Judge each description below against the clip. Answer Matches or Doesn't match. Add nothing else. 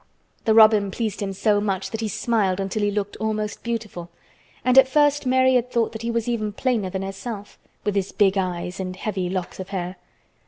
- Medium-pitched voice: Doesn't match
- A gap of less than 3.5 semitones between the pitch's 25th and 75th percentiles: Matches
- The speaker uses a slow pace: Doesn't match